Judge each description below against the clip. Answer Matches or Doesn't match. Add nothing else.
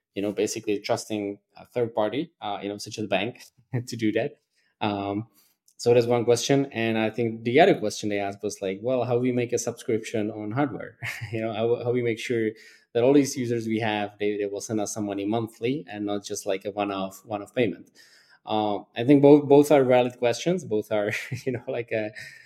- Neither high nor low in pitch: Doesn't match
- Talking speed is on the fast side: Matches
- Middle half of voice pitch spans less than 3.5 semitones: Matches